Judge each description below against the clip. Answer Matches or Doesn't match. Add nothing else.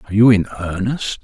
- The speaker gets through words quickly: Doesn't match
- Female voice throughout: Doesn't match